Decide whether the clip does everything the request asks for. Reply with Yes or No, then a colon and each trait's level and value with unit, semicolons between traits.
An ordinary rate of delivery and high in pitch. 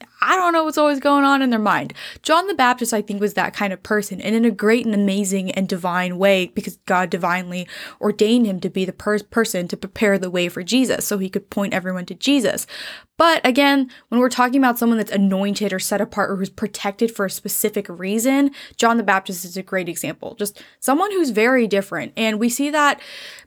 No: fast, 220 wpm; high, 210 Hz